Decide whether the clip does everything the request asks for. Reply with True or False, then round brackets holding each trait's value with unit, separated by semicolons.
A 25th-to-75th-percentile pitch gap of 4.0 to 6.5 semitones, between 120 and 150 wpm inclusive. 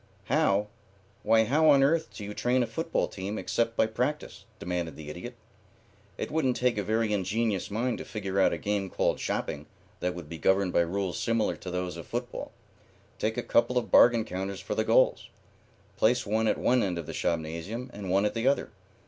False (4.4 semitones; 200 wpm)